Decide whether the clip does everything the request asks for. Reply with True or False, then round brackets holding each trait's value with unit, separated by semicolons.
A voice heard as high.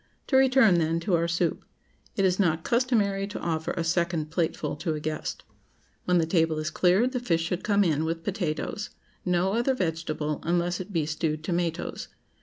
False (170 Hz)